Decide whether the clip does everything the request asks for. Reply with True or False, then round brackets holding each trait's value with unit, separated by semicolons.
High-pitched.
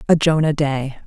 False (145 Hz)